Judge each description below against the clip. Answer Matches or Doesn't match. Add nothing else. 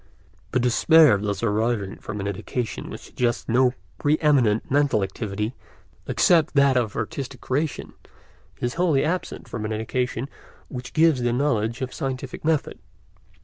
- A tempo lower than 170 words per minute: Matches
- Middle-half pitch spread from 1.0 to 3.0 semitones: Doesn't match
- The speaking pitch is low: Matches